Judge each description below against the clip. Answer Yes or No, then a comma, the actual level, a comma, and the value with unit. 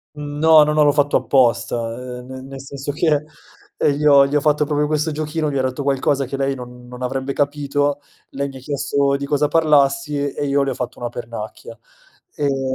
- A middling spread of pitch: No, narrow, 1.9 semitones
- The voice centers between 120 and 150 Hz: Yes, medium, 140 Hz